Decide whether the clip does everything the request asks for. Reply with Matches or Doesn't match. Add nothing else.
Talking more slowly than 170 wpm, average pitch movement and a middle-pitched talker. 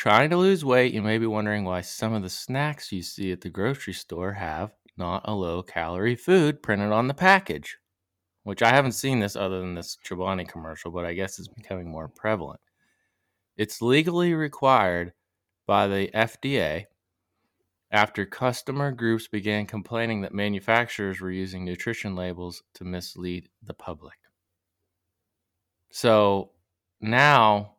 Doesn't match